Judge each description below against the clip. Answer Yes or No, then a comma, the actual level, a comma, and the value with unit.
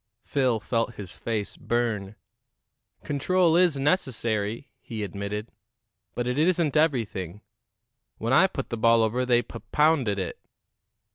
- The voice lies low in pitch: Yes, low, 120 Hz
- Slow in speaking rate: Yes, slow, 130 wpm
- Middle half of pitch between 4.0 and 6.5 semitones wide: Yes, average, 5.1 semitones